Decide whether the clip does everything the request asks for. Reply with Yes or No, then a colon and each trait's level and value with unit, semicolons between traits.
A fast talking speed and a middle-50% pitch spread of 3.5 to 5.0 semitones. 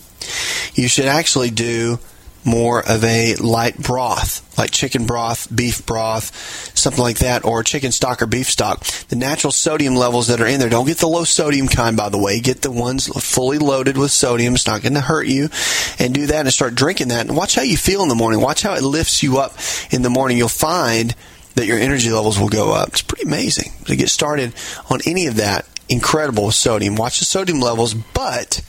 No: fast, 220 wpm; average, 3.1 semitones